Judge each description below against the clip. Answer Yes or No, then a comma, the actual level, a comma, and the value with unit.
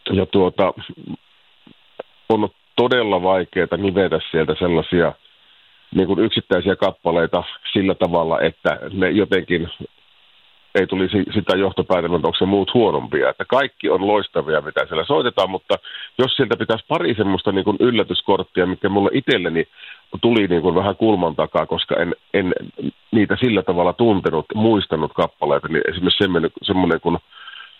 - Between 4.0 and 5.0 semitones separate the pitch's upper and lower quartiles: No, average, 3.5 semitones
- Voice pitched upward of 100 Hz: No, very low, 95 Hz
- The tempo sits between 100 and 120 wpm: No, average, 130 wpm